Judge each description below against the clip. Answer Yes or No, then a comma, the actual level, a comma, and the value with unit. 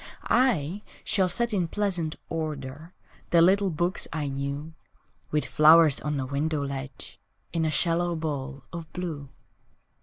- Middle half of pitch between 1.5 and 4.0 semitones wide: Yes, average, 3.5 semitones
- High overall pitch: No, medium, 160 Hz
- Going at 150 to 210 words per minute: No, average, 140 wpm